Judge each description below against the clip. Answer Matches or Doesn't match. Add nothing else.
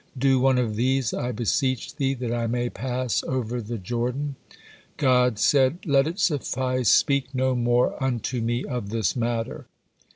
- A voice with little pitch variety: Matches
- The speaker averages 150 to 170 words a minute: Matches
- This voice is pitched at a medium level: Doesn't match